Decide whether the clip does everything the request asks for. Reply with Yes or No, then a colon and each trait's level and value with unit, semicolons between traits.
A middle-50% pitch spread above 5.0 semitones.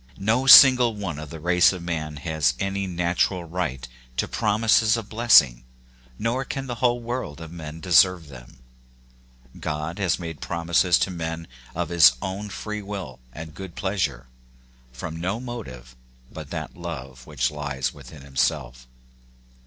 Yes: wide, 5.4 semitones